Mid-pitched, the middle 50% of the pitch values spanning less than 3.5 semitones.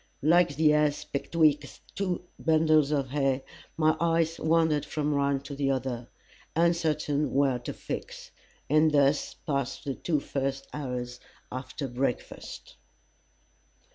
Yes: medium, 145 Hz; narrow, 2.5 semitones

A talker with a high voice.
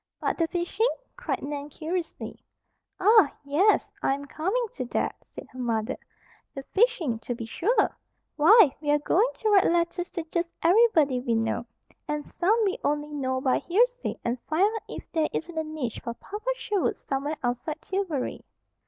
Yes: very high, 320 Hz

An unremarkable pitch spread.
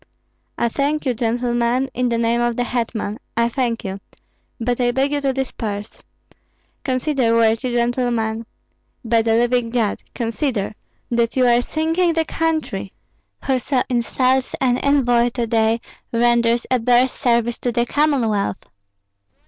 No: narrow, 2.0 semitones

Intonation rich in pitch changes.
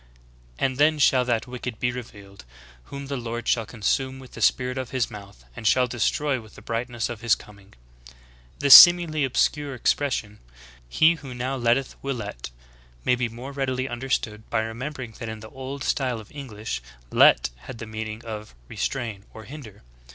No: average, 3.4 semitones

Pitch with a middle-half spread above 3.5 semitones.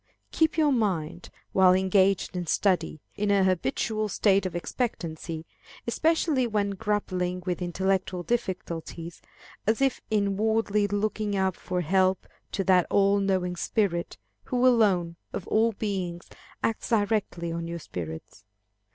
No: average, 3.2 semitones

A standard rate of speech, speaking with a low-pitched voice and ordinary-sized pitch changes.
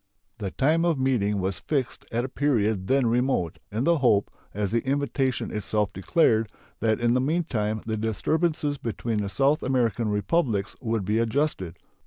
Yes: average, 165 wpm; low, 115 Hz; average, 4.6 semitones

